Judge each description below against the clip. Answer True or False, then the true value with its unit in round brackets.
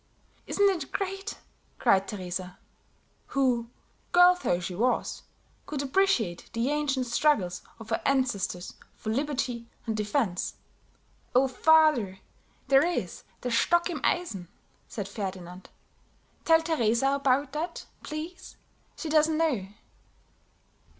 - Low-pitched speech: False (260 Hz)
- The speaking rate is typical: False (115 wpm)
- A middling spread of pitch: False (6.9 semitones)